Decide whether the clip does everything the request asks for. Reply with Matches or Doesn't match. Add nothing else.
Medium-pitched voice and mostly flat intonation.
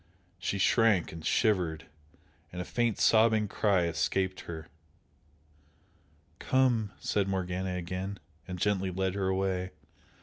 Doesn't match